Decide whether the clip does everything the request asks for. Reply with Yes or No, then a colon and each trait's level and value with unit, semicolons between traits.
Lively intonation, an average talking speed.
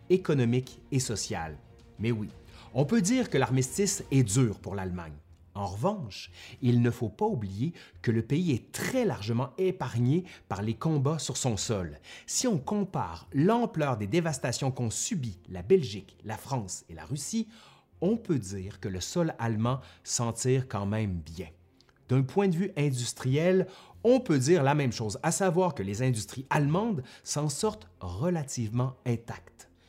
Yes: wide, 7.3 semitones; average, 165 wpm